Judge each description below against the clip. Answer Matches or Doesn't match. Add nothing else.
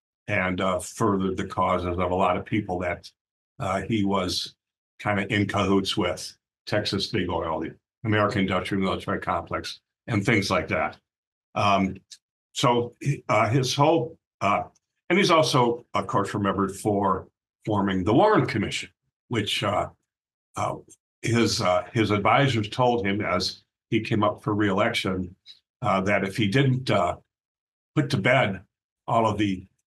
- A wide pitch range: Doesn't match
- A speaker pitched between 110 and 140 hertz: Doesn't match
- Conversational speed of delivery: Matches